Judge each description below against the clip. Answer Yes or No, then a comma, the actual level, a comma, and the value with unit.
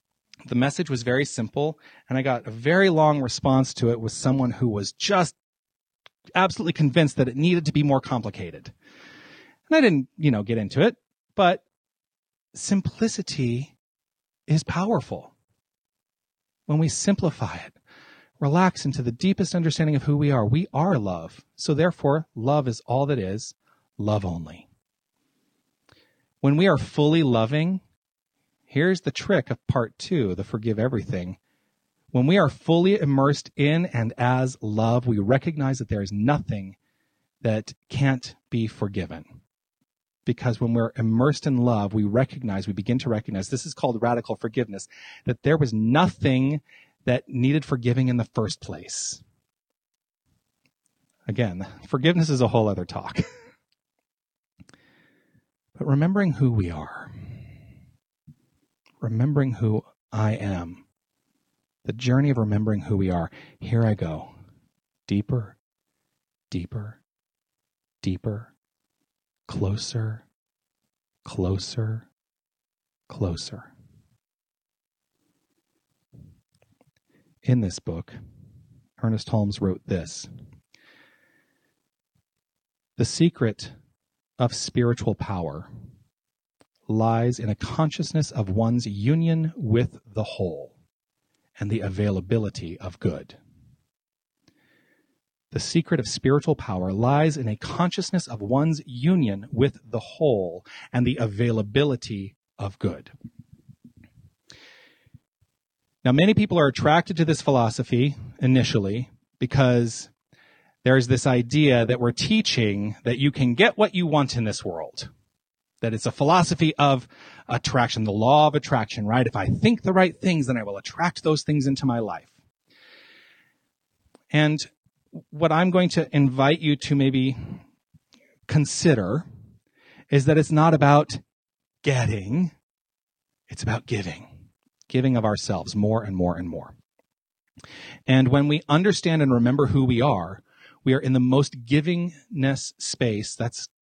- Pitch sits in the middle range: No, low, 130 Hz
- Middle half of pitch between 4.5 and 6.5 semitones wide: Yes, average, 5.1 semitones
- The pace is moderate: No, slow, 125 wpm